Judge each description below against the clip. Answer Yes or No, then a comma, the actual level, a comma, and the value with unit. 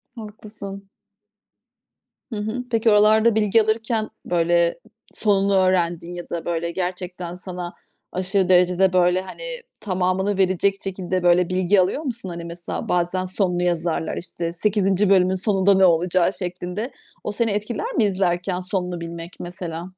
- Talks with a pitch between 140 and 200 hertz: Yes, medium, 185 Hz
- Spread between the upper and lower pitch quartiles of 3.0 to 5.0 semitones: No, narrow, 2.4 semitones